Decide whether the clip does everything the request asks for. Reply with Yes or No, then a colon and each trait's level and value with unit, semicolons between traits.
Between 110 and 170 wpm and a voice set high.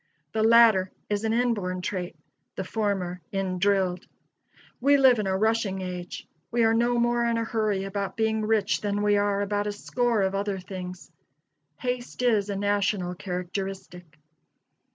Yes: average, 160 wpm; high, 205 Hz